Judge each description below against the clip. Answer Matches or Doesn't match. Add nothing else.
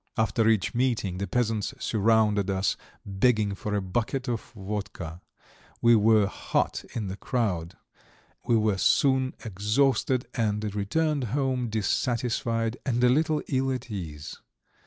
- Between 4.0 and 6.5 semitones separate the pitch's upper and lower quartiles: Doesn't match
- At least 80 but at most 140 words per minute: Matches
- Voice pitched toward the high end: Doesn't match